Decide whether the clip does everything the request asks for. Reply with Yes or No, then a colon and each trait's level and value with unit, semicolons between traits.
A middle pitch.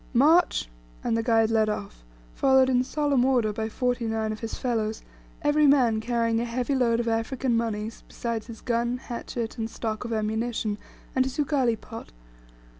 No: high, 235 Hz